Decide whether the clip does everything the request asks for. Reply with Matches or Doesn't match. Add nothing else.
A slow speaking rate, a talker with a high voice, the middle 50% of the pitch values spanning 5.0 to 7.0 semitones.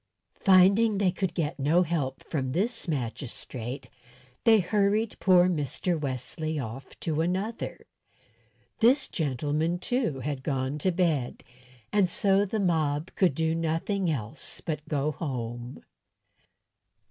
Doesn't match